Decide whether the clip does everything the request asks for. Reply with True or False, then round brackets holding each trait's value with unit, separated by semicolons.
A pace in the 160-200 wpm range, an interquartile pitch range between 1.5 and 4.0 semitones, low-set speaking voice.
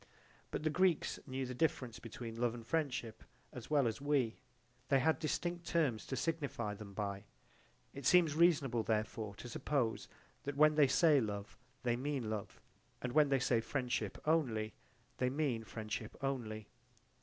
False (165 wpm; 4.8 semitones; 130 Hz)